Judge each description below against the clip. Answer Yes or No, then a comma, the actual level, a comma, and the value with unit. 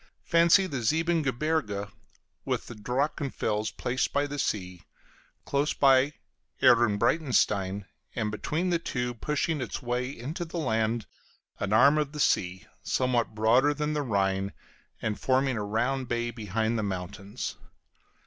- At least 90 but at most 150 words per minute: Yes, slow, 135 wpm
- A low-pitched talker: Yes, low, 125 Hz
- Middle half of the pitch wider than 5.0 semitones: Yes, wide, 5.4 semitones